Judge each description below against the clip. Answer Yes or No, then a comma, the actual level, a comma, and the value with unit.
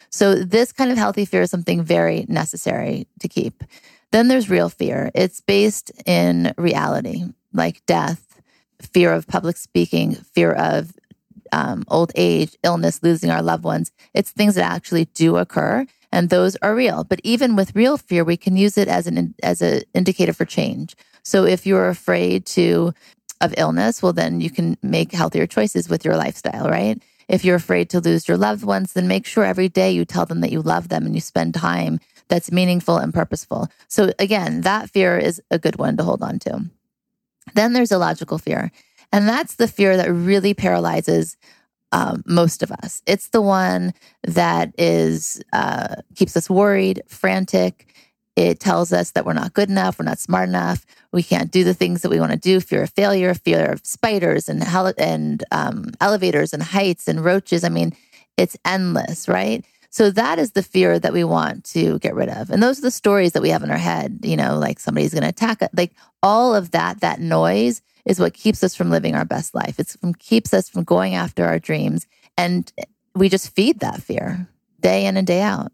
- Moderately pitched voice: Yes, medium, 175 Hz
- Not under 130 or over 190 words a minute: No, average, 200 wpm